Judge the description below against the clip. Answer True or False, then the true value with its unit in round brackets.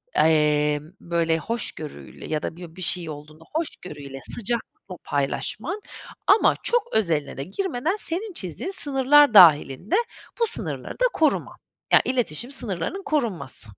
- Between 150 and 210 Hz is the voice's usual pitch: True (185 Hz)